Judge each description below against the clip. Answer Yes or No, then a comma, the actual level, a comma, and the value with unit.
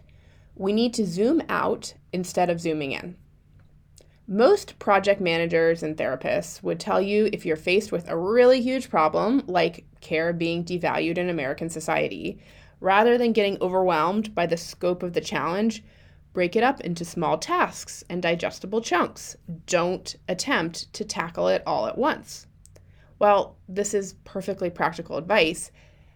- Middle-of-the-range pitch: Yes, medium, 175 Hz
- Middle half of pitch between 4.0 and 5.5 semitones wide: Yes, average, 4.3 semitones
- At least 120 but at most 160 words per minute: Yes, average, 150 wpm